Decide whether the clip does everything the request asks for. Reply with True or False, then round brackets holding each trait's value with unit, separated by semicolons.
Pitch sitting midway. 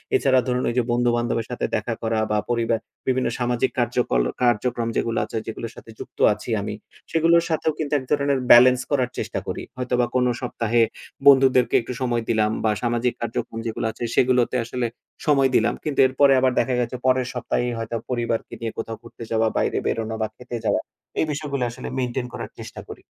False (120 Hz)